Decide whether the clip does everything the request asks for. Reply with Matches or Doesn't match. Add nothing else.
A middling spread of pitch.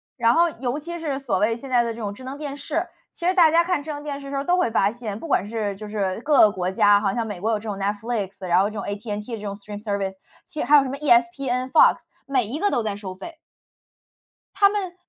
Doesn't match